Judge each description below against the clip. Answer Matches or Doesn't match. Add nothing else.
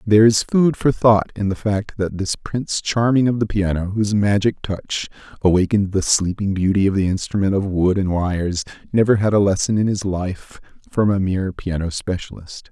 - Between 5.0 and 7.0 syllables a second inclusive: Matches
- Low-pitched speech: Matches